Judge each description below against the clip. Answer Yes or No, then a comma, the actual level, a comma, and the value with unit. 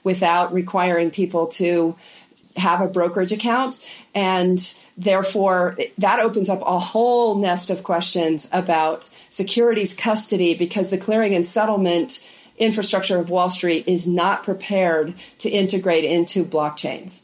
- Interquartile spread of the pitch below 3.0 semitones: Yes, narrow, 2.6 semitones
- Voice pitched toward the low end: No, medium, 185 Hz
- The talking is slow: Yes, slow, 130 wpm